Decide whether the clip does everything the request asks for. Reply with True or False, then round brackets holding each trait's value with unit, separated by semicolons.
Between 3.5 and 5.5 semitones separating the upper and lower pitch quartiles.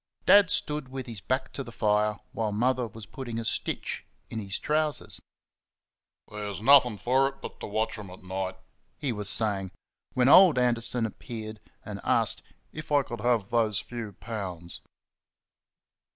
True (3.8 semitones)